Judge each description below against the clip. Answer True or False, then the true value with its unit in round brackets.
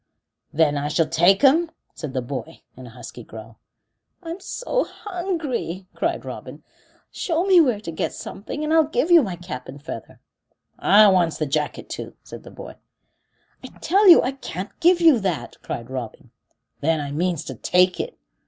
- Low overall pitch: False (180 Hz)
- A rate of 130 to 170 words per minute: False (180 wpm)